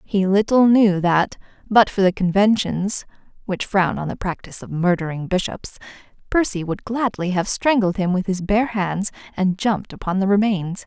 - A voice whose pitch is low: No, high, 195 Hz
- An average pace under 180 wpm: Yes, average, 170 wpm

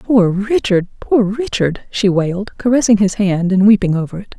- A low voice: No, high, 205 Hz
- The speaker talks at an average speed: Yes, average, 180 wpm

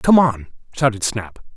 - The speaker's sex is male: Yes, male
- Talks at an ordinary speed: Yes, average, 155 wpm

